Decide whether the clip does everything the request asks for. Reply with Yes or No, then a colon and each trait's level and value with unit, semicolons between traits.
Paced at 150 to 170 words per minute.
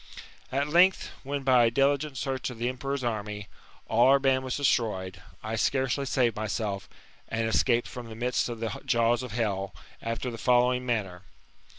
Yes: average, 160 wpm